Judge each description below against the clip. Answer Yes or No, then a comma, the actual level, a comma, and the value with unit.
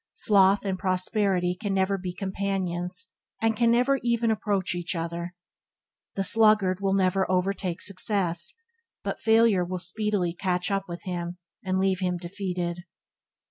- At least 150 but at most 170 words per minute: No, average, 140 wpm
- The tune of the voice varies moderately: No, narrow, 2.2 semitones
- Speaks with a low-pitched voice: No, high, 190 Hz